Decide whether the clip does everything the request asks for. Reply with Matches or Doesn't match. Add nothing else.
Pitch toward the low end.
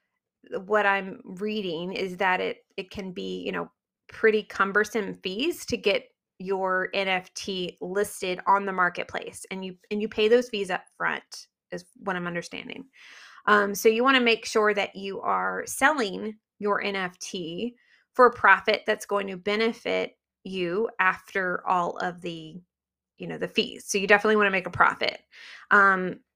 Doesn't match